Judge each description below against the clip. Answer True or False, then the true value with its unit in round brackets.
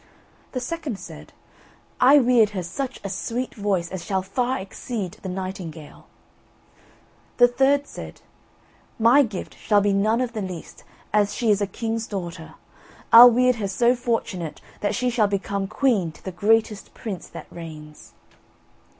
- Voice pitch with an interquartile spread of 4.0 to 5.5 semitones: True (4.3 semitones)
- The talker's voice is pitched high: True (210 Hz)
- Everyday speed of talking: True (155 wpm)